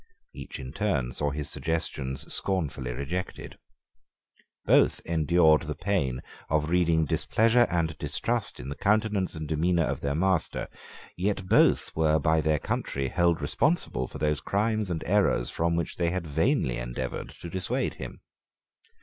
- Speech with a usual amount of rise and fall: Yes, average, 4.2 semitones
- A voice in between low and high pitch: No, very low, 80 Hz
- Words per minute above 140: Yes, average, 150 wpm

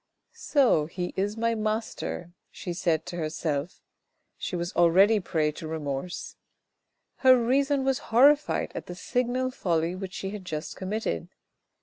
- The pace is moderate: Yes, average, 145 wpm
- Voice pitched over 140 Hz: Yes, high, 190 Hz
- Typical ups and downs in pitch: No, wide, 5.9 semitones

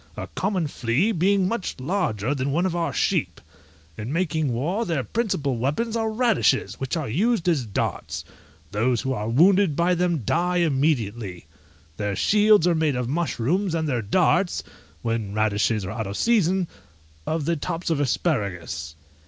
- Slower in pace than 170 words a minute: Yes, average, 160 wpm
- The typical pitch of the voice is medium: Yes, medium, 155 Hz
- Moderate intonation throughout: No, wide, 7.5 semitones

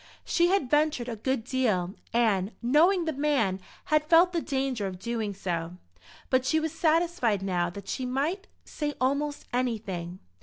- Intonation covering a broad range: Yes, wide, 7.1 semitones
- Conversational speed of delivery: Yes, average, 160 wpm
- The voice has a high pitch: Yes, very high, 255 Hz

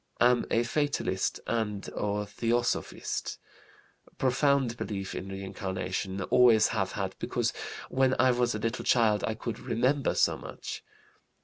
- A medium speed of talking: No, slow, 130 wpm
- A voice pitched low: Yes, low, 115 Hz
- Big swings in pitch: No, average, 3.4 semitones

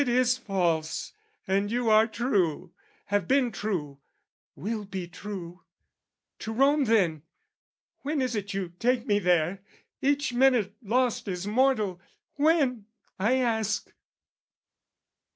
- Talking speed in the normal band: No, slow, 120 wpm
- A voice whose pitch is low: No, high, 215 Hz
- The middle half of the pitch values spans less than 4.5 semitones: No, average, 4.9 semitones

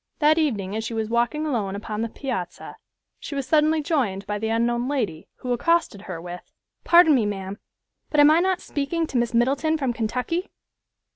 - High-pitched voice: Yes, high, 245 Hz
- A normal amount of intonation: No, wide, 6.2 semitones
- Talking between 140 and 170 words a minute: No, average, 190 wpm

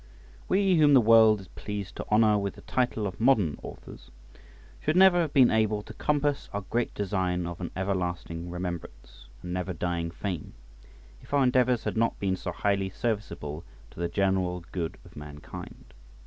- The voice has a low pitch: Yes, low, 100 Hz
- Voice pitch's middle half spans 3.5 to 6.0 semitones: Yes, average, 4.6 semitones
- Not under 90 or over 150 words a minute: No, average, 175 wpm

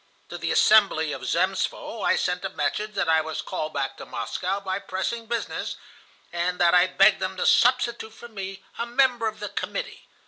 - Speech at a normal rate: Yes, average, 195 wpm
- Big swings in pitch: No, average, 4.1 semitones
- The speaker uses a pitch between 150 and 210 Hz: Yes, high, 190 Hz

